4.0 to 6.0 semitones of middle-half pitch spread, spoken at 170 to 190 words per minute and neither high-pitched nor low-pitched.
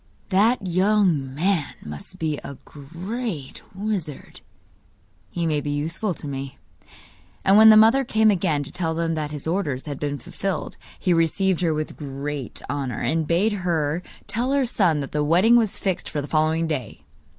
Yes: average, 5.1 semitones; average, 175 wpm; medium, 165 Hz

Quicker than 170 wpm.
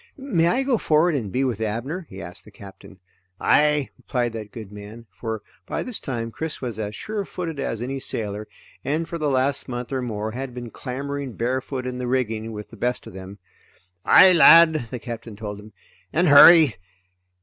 Yes: average, 190 wpm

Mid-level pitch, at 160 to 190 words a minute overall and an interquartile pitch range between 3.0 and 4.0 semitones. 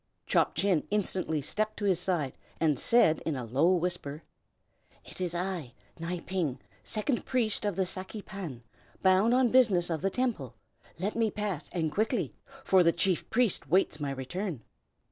No: medium, 180 Hz; average, 165 wpm; average, 4.6 semitones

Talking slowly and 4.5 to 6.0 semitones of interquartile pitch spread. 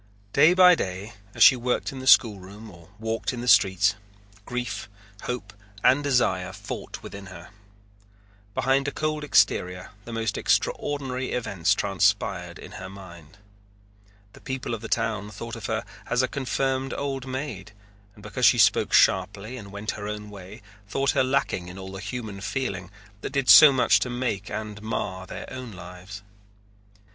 No: average, 165 wpm; average, 4.9 semitones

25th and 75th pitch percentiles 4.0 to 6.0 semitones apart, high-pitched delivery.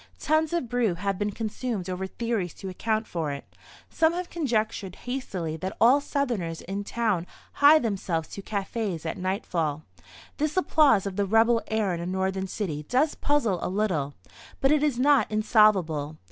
Yes: average, 5.3 semitones; high, 210 Hz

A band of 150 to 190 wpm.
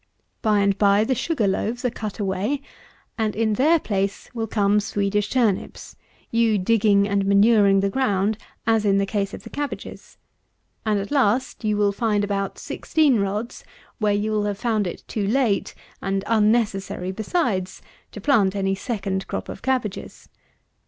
Yes: average, 165 wpm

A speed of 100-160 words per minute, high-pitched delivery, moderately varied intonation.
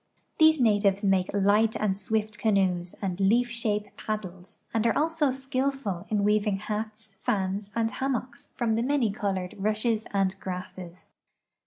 Yes: average, 150 wpm; high, 210 Hz; average, 3.1 semitones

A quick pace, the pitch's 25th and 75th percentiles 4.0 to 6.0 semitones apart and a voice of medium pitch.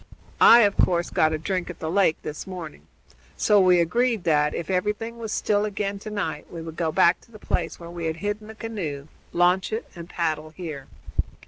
Yes: fast, 210 wpm; average, 4.4 semitones; medium, 180 Hz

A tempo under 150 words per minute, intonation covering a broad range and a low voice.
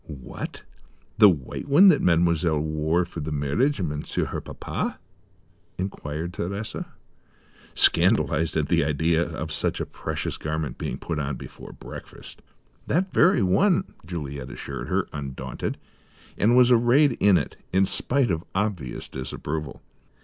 Yes: average, 140 wpm; wide, 5.7 semitones; very low, 85 Hz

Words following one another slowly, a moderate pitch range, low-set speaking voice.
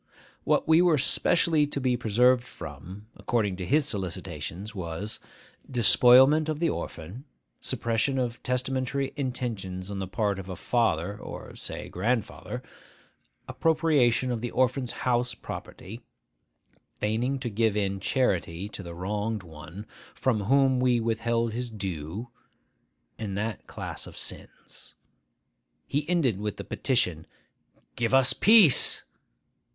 Yes: slow, 130 wpm; average, 4.8 semitones; low, 115 Hz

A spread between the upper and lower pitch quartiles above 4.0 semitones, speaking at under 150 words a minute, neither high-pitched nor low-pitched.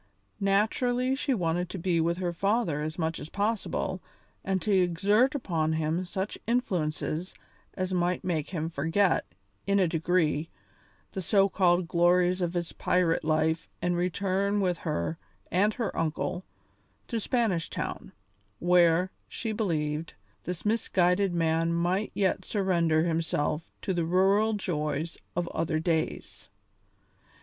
No: average, 3.1 semitones; slow, 135 wpm; medium, 180 Hz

